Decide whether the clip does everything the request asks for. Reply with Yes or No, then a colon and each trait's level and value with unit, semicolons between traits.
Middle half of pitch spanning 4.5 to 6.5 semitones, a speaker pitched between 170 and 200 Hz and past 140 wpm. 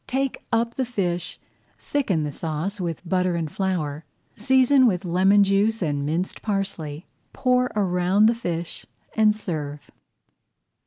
No: average, 4.8 semitones; high, 190 Hz; slow, 135 wpm